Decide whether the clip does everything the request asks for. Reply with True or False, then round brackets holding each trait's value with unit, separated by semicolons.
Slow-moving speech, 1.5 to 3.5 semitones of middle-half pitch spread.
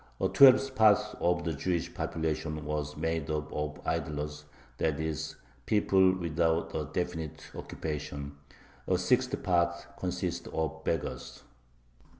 True (125 wpm; 2.5 semitones)